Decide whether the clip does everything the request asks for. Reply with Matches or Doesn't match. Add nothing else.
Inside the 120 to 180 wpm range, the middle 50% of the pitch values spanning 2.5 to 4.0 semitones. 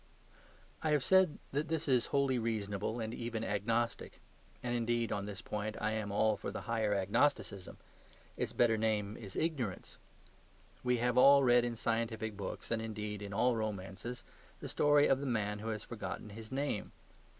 Matches